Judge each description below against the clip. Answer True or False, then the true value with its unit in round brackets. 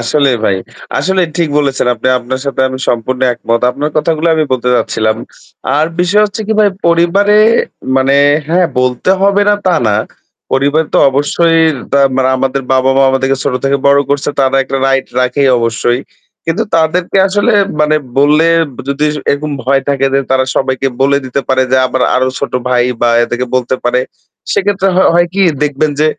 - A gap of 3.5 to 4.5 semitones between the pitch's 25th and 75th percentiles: True (4.0 semitones)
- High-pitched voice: False (140 Hz)